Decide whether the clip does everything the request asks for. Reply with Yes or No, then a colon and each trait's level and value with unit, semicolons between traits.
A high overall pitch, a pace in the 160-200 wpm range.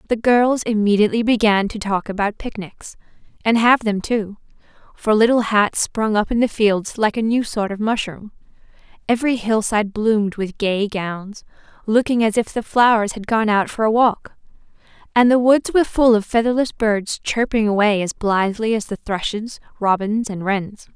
Yes: high, 215 Hz; average, 170 wpm